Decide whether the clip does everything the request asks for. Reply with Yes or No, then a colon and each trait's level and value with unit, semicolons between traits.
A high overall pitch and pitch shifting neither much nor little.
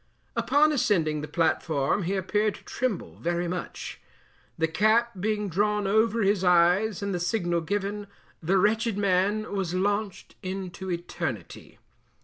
Yes: high, 195 Hz; average, 3.3 semitones